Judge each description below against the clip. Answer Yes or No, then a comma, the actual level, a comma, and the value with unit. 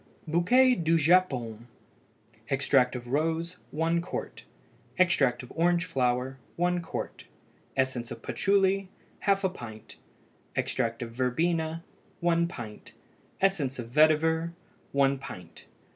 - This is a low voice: No, medium, 160 Hz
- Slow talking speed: Yes, slow, 110 wpm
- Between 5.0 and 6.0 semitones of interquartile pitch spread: Yes, wide, 5.5 semitones